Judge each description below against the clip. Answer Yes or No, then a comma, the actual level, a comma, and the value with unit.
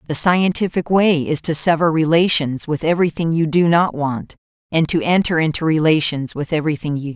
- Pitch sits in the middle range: Yes, medium, 160 Hz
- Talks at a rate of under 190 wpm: No, average, 195 wpm